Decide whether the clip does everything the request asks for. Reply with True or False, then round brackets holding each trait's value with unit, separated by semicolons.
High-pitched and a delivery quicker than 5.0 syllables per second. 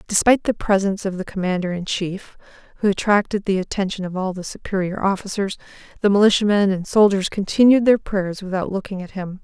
True (195 Hz; 6.0 syllables/s)